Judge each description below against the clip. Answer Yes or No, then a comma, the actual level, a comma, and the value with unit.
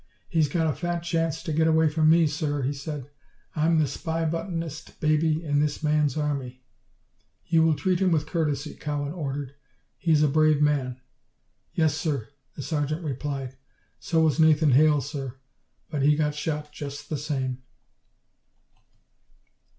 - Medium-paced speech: Yes, average, 160 wpm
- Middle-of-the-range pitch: Yes, medium, 150 Hz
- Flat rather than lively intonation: Yes, narrow, 2.0 semitones